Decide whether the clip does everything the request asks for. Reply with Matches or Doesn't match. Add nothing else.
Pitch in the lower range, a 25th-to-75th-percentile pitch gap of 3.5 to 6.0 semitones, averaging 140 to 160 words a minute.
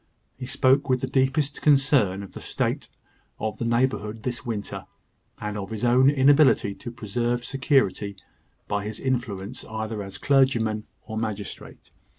Matches